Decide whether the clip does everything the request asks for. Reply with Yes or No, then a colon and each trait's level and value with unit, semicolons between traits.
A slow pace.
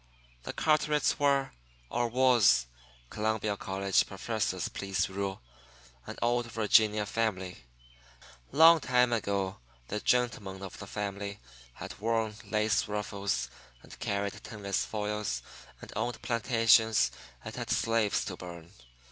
Yes: slow, 120 wpm